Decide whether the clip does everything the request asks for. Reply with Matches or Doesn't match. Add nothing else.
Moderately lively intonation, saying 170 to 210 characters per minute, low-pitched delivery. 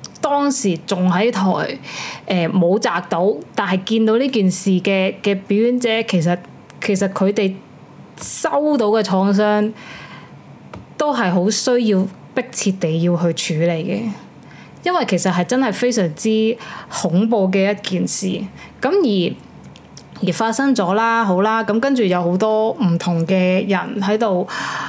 Doesn't match